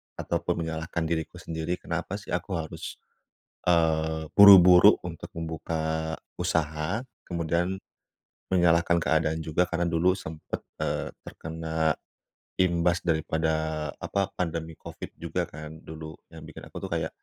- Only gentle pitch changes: Yes, narrow, 1.6 semitones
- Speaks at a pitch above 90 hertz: No, very low, 80 Hz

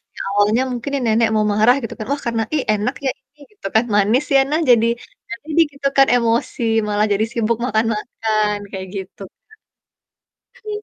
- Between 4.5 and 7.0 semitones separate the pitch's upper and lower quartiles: No, average, 3.4 semitones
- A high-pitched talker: Yes, high, 230 Hz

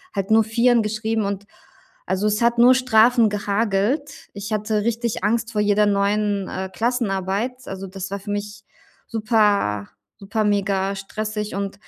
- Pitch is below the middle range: No, high, 210 Hz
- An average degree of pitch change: No, narrow, 2.2 semitones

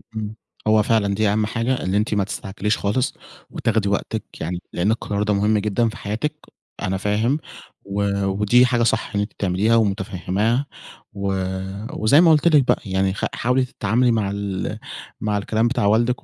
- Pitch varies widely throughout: No, average, 2.7 semitones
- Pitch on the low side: Yes, low, 105 Hz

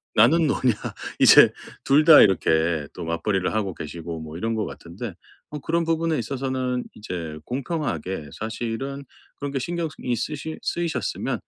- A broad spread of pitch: Yes, wide, 8.5 semitones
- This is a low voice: Yes, low, 120 Hz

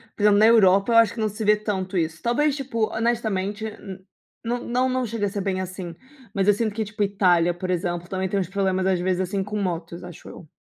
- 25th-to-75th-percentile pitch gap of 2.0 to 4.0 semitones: Yes, average, 2.9 semitones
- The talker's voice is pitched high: Yes, high, 200 Hz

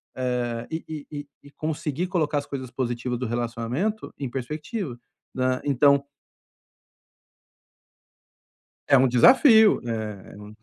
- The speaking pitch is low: Yes, low, 130 Hz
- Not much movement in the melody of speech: No, average, 4.0 semitones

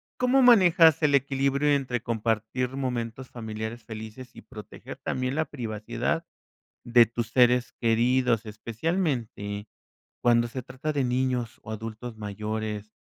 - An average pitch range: Yes, average, 3.4 semitones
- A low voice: Yes, low, 120 Hz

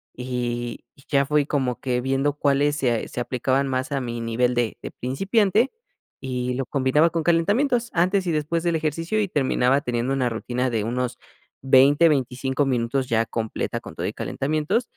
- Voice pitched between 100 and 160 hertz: Yes, low, 135 Hz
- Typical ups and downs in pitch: Yes, average, 3.7 semitones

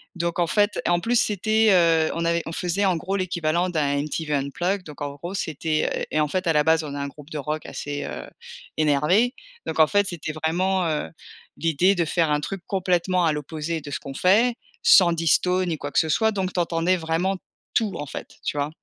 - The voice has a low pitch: No, medium, 170 Hz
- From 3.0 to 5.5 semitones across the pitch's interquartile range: Yes, average, 3.4 semitones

